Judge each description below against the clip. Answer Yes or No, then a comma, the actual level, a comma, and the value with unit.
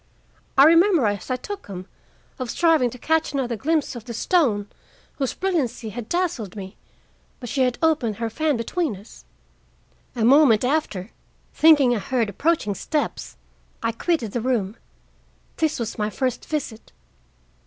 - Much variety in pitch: Yes, wide, 6.0 semitones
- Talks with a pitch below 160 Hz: No, very high, 250 Hz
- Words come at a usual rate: Yes, average, 155 wpm